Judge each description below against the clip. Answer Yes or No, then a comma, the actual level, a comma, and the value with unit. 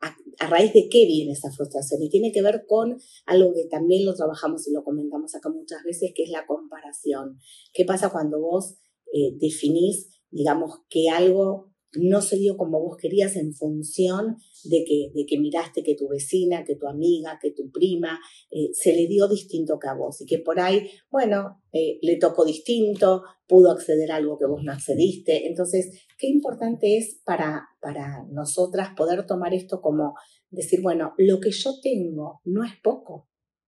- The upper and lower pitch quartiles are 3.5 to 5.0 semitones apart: Yes, average, 4.2 semitones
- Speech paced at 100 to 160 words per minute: No, average, 185 wpm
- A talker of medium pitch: Yes, medium, 175 Hz